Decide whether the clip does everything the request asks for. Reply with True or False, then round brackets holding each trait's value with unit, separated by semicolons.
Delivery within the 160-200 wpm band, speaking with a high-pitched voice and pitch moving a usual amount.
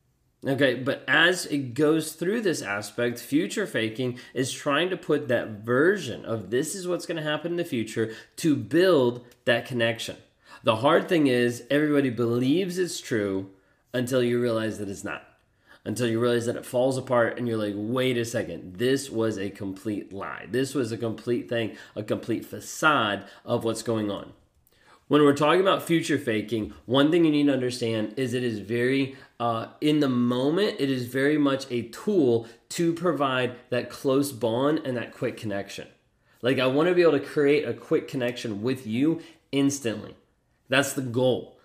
False (180 wpm; 125 Hz; 3.6 semitones)